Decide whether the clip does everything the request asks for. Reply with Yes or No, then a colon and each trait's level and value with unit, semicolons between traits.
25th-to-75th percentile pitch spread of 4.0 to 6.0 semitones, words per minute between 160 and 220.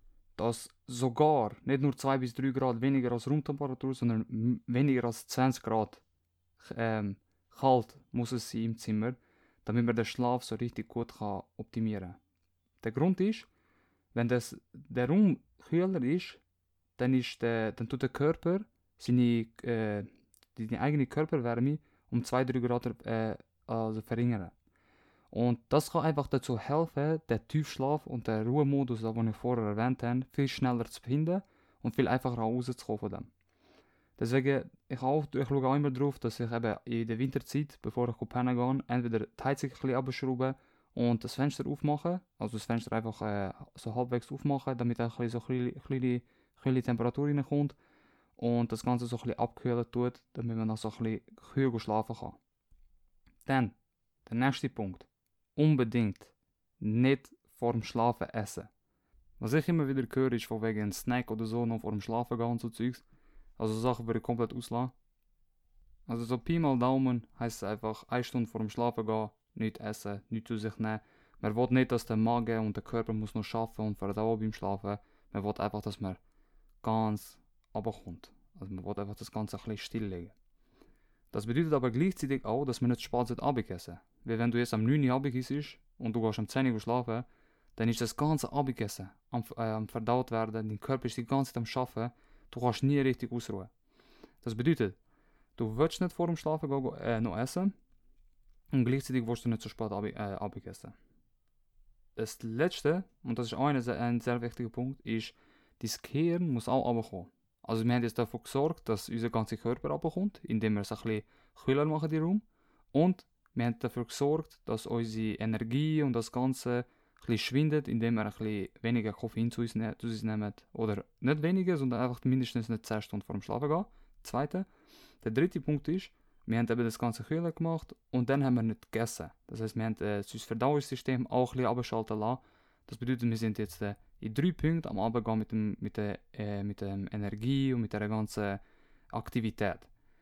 No: average, 3.1 semitones; average, 180 wpm